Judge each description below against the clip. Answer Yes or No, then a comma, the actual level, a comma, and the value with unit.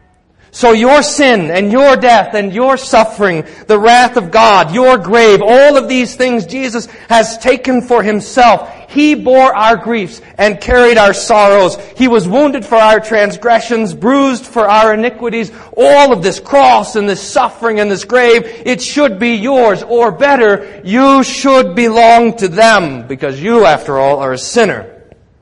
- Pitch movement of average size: Yes, average, 3.5 semitones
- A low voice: No, high, 230 Hz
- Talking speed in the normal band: Yes, average, 165 wpm